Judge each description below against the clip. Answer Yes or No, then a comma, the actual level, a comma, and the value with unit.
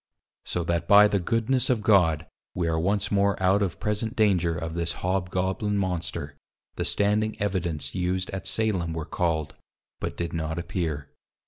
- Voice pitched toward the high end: No, very low, 90 Hz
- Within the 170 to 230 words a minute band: No, average, 160 wpm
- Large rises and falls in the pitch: No, average, 3.6 semitones